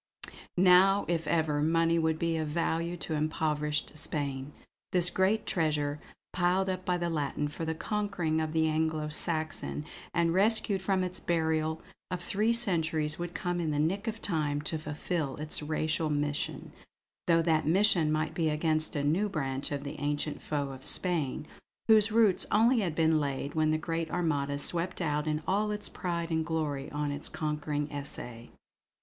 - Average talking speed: Yes, average, 170 wpm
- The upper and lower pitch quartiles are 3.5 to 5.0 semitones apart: No, average, 2.9 semitones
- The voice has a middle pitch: Yes, medium, 160 Hz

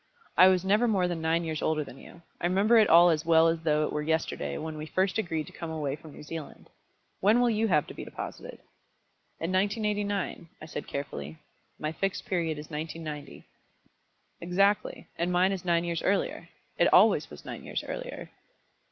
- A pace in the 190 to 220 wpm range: Yes, average, 195 wpm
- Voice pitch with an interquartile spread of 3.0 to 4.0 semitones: Yes, average, 3.7 semitones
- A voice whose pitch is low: No, medium, 170 Hz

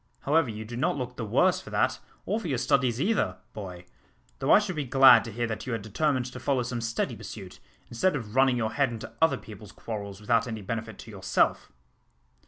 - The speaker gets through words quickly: Yes, fast, 215 wpm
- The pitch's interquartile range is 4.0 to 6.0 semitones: No, average, 3.5 semitones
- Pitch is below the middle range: Yes, low, 120 Hz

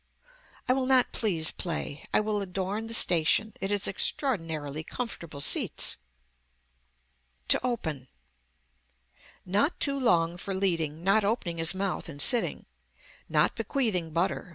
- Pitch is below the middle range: No, high, 190 Hz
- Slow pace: Yes, slow, 130 wpm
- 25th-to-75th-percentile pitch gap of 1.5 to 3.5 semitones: No, average, 5.2 semitones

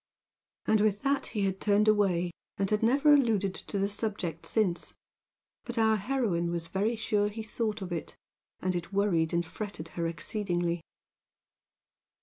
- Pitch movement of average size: Yes, average, 3.9 semitones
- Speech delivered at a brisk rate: No, average, 155 wpm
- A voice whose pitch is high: Yes, high, 200 Hz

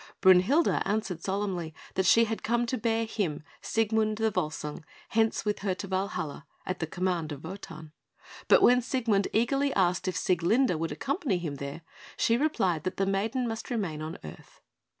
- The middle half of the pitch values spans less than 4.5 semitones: No, average, 5.0 semitones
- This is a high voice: Yes, high, 195 Hz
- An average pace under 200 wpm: Yes, average, 170 wpm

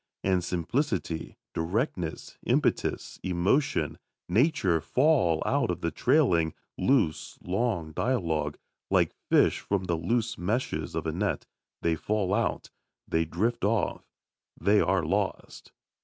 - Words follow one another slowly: Yes, slow, 120 wpm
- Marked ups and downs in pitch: Yes, wide, 6.1 semitones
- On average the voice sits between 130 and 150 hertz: No, very low, 95 Hz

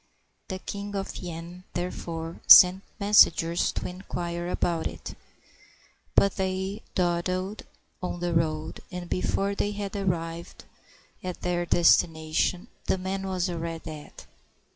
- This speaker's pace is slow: Yes, slow, 120 wpm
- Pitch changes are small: Yes, narrow, 2.2 semitones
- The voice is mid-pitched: Yes, medium, 180 Hz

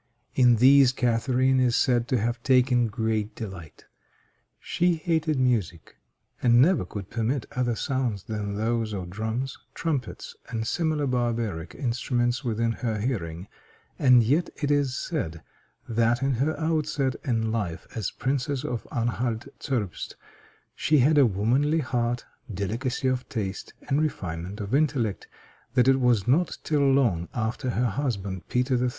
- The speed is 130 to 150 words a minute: Yes, average, 145 wpm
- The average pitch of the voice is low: Yes, low, 120 Hz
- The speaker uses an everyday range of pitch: Yes, average, 3.4 semitones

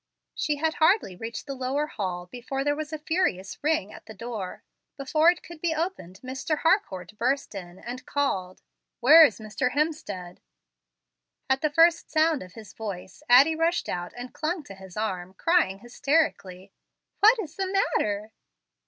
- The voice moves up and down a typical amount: No, wide, 8.2 semitones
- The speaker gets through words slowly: No, average, 165 wpm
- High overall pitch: Yes, very high, 265 Hz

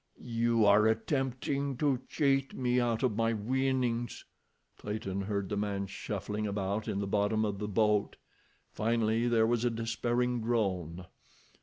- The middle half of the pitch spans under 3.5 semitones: Yes, average, 2.9 semitones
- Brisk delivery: No, average, 145 wpm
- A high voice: No, low, 110 Hz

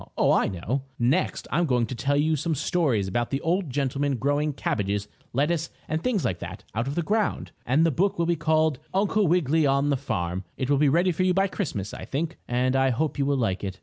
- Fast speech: Yes, fast, 235 wpm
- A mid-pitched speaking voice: Yes, medium, 145 Hz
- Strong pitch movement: No, average, 4.9 semitones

